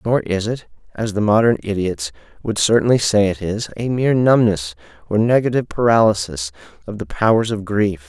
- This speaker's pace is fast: No, average, 170 wpm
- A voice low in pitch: Yes, low, 105 Hz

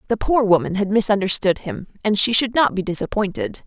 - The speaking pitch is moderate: No, high, 200 Hz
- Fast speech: No, average, 195 wpm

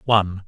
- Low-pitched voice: Yes, low, 100 Hz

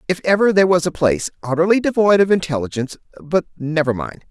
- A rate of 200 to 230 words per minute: No, average, 180 wpm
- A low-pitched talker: No, medium, 165 Hz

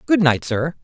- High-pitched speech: No, medium, 155 Hz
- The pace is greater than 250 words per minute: No, fast, 215 wpm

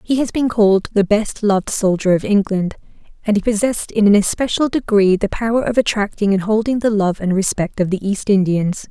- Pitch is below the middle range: No, high, 205 Hz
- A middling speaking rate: No, fast, 210 wpm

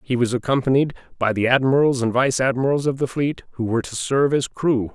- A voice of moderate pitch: No, low, 130 Hz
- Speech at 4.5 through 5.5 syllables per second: No, 6.0 syllables/s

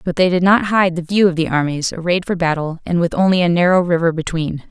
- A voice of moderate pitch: Yes, medium, 175 Hz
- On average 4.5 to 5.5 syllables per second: No, 6.0 syllables/s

